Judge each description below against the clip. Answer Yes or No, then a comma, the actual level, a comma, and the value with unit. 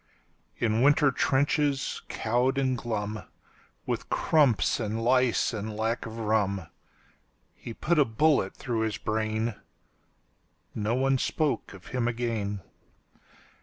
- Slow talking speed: Yes, slow, 105 wpm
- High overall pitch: No, low, 115 Hz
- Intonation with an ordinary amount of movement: Yes, average, 3.5 semitones